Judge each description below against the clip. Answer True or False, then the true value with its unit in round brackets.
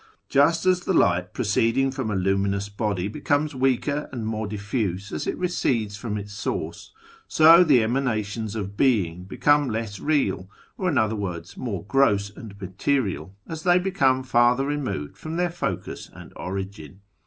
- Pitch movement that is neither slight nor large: False (5.9 semitones)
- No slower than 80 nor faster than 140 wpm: False (160 wpm)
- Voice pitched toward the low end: True (110 Hz)